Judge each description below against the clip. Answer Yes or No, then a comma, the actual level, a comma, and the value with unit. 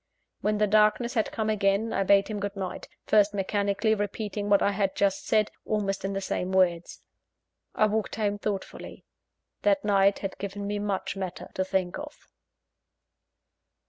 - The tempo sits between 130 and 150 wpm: No, average, 165 wpm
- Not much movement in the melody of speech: Yes, narrow, 1.5 semitones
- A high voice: Yes, high, 200 Hz